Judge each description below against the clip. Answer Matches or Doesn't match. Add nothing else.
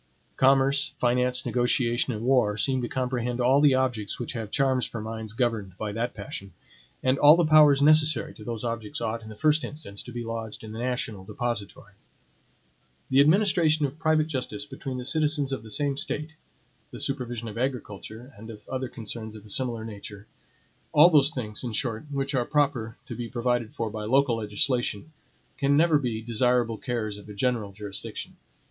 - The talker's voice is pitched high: Doesn't match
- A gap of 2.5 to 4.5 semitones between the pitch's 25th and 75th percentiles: Matches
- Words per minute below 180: Doesn't match